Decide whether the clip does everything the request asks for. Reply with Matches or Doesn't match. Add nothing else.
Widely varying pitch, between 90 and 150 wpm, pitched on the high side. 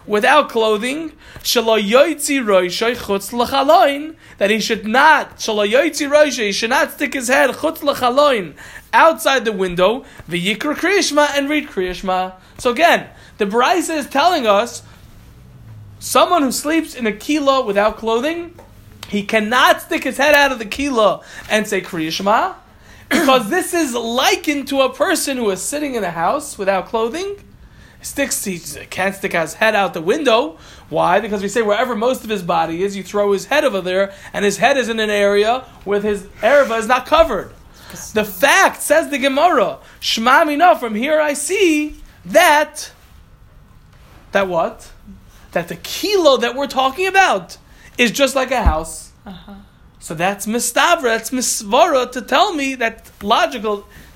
Matches